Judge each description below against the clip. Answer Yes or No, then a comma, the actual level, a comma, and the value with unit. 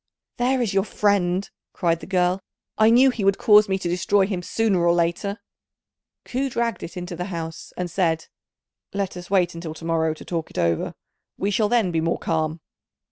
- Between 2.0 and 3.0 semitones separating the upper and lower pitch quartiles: No, average, 3.5 semitones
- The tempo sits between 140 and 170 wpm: No, average, 195 wpm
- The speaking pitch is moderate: Yes, medium, 180 Hz